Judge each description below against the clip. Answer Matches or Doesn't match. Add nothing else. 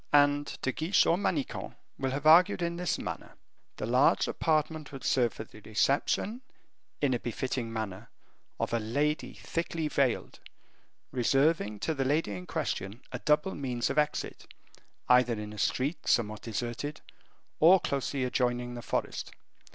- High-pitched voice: Doesn't match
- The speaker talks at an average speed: Matches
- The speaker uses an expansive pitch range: Doesn't match